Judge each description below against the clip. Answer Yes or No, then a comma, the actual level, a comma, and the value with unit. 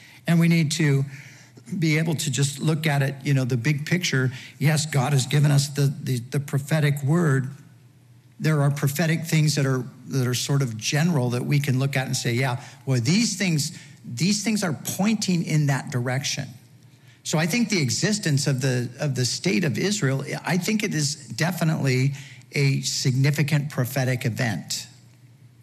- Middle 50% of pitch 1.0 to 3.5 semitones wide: Yes, average, 3.2 semitones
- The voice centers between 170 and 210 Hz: No, medium, 140 Hz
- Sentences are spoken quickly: No, average, 180 wpm